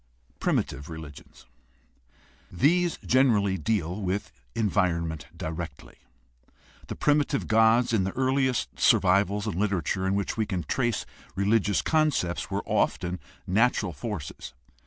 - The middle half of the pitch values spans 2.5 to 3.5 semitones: No, average, 4.8 semitones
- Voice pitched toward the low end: Yes, low, 100 Hz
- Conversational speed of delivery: No, slow, 120 wpm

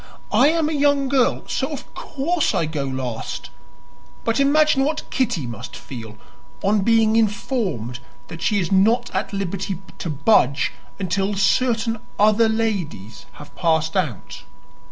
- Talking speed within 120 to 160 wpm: Yes, average, 140 wpm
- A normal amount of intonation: No, wide, 7.5 semitones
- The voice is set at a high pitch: Yes, high, 200 Hz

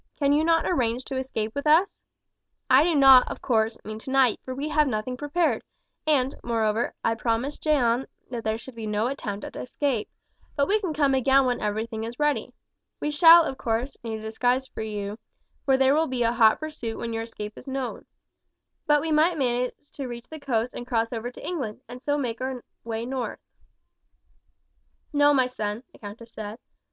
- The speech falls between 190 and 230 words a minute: Yes, average, 195 wpm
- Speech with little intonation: No, average, 3.9 semitones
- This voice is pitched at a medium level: No, very high, 250 Hz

